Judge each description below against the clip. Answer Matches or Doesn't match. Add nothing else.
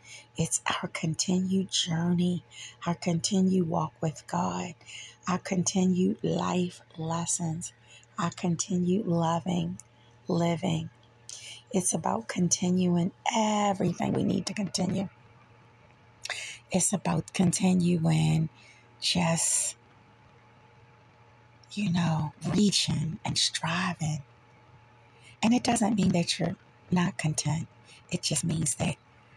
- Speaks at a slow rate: Matches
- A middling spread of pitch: Doesn't match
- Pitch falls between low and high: Matches